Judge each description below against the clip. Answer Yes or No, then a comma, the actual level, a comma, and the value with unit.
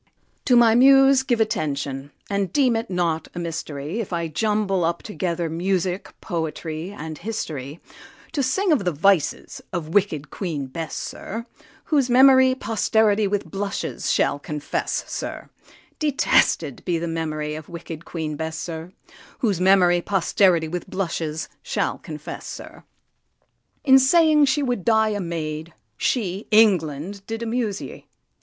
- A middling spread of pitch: No, wide, 5.8 semitones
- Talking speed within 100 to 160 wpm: Yes, average, 140 wpm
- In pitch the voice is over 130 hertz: Yes, medium, 185 Hz